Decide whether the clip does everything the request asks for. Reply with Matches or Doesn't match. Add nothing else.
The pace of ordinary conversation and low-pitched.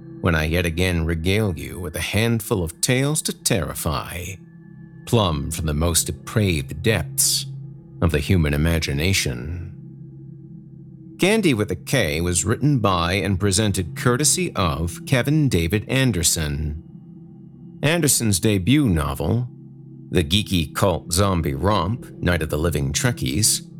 Doesn't match